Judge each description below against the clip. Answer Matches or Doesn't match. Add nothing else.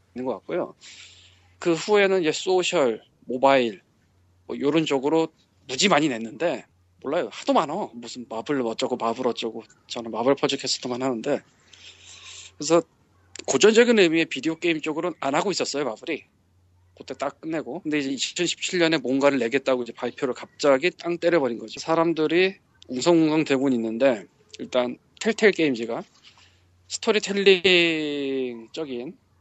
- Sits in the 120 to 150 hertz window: Matches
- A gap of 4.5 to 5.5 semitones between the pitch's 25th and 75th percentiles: Doesn't match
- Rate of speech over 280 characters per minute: Matches